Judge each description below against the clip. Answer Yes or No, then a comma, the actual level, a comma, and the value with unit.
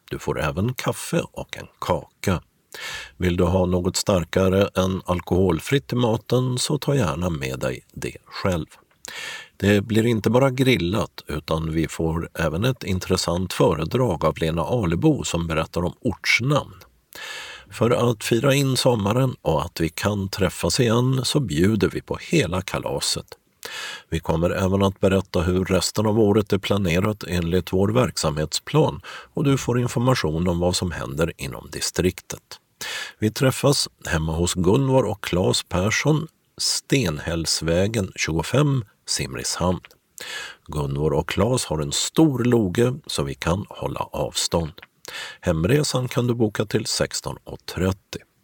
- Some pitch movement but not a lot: No, wide, 6.1 semitones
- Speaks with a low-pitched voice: Yes, very low, 95 Hz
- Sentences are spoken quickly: No, average, 140 wpm